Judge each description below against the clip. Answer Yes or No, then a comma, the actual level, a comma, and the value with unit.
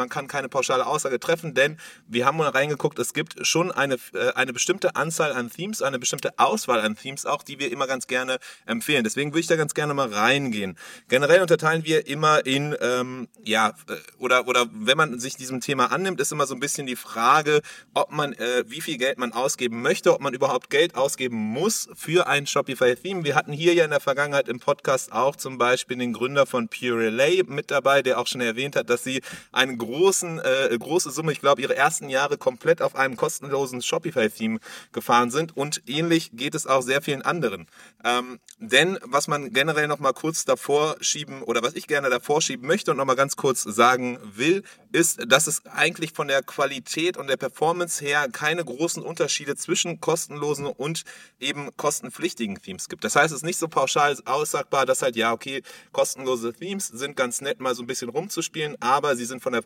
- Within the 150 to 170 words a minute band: No, fast, 205 wpm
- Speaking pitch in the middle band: Yes, medium, 145 Hz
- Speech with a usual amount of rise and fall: Yes, average, 4.4 semitones